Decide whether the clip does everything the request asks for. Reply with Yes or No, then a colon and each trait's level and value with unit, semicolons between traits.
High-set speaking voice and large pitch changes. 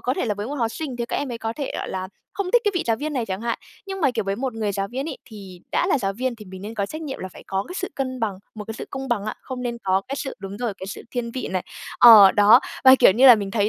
No: high, 230 Hz; average, 4.7 semitones